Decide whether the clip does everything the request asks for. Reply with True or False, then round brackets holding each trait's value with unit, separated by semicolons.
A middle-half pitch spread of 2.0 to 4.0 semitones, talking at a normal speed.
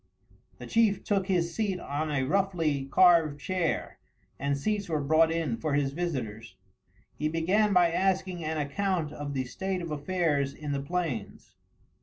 False (4.6 semitones; 160 wpm)